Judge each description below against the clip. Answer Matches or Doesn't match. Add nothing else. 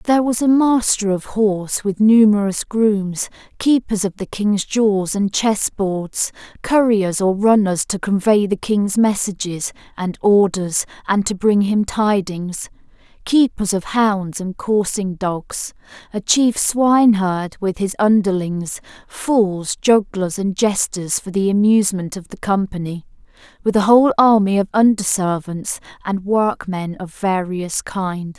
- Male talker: Doesn't match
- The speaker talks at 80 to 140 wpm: Matches